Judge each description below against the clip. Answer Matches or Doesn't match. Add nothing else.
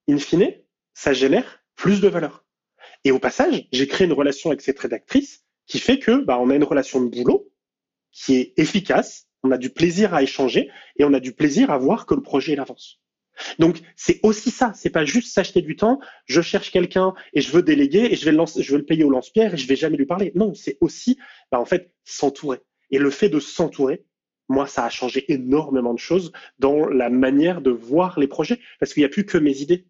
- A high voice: Doesn't match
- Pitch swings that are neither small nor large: Doesn't match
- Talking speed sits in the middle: Doesn't match